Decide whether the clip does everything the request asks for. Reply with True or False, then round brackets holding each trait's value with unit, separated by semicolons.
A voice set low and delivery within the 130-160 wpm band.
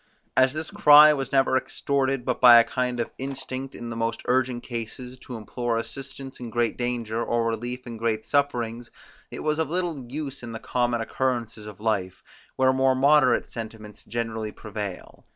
False (120 Hz; 175 wpm)